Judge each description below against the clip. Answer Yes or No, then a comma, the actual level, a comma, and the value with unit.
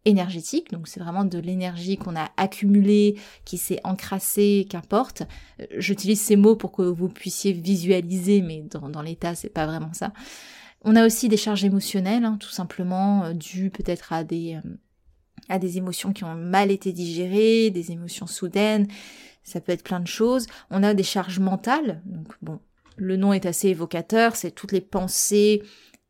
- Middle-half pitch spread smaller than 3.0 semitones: Yes, narrow, 2.6 semitones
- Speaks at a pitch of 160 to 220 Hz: Yes, high, 190 Hz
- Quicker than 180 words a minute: No, average, 170 wpm